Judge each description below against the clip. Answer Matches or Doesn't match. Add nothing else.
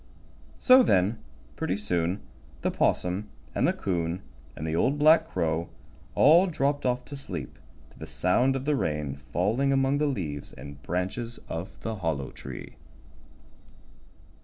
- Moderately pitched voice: Doesn't match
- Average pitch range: Doesn't match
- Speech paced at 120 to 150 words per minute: Matches